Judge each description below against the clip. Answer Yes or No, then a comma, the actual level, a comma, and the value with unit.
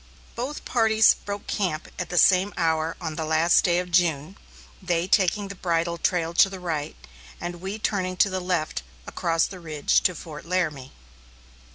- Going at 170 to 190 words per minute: Yes, average, 175 wpm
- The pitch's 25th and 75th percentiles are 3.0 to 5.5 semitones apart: No, narrow, 2.6 semitones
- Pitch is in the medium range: Yes, medium, 175 Hz